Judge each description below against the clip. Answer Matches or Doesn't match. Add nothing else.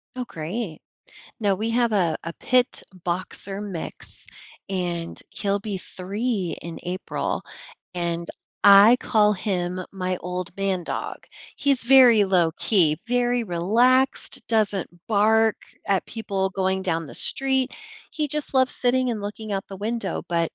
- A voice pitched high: Matches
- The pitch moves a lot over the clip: Doesn't match